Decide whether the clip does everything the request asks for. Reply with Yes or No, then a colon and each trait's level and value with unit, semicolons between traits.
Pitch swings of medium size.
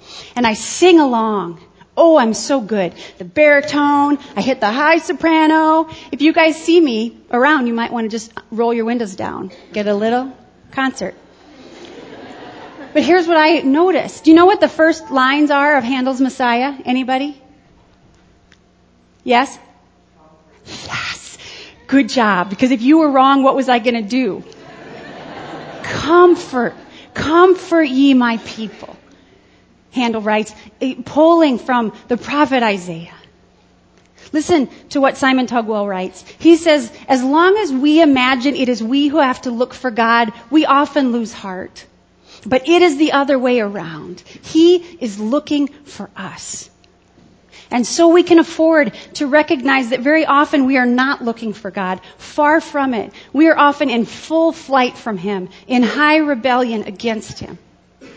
Yes: average, 4.6 semitones